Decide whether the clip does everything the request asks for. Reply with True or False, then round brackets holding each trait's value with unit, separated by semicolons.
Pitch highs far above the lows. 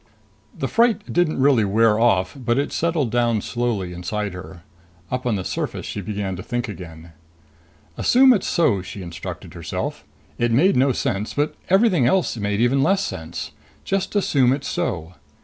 True (6.8 semitones)